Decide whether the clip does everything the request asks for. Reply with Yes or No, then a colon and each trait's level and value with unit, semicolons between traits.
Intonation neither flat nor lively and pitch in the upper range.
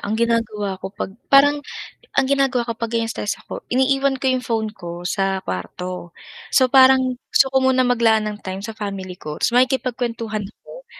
Yes: average, 4.6 semitones; high, 230 Hz